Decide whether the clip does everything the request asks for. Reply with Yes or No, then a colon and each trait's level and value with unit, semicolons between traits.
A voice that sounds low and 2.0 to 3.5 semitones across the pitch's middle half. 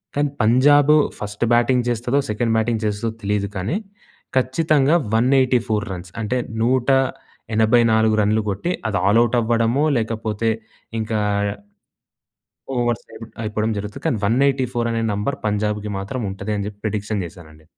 Yes: low, 115 Hz; average, 3.2 semitones